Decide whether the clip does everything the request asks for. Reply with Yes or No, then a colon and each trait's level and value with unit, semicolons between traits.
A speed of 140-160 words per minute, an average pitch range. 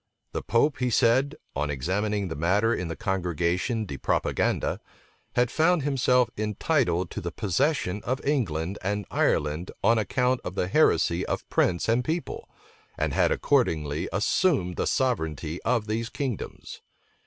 No: average, 145 wpm; wide, 6.4 semitones